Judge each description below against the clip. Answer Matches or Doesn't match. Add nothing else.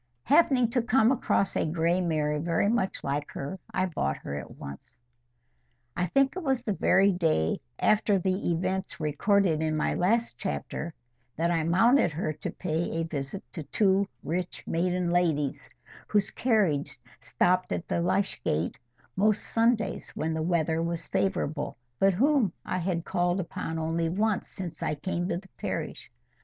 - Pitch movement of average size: Matches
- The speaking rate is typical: Matches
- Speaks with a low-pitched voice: Doesn't match